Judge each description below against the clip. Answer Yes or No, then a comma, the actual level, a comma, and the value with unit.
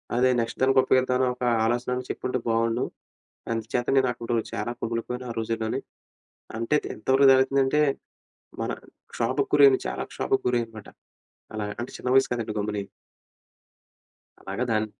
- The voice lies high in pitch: No, low, 125 Hz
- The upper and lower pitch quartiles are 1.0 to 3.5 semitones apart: Yes, narrow, 2.5 semitones